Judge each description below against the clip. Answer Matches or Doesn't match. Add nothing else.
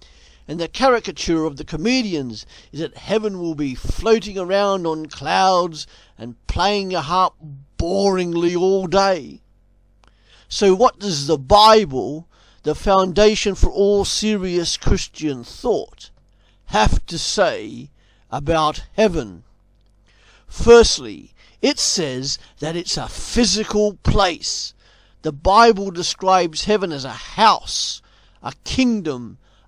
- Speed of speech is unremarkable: Doesn't match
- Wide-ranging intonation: Matches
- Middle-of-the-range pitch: Matches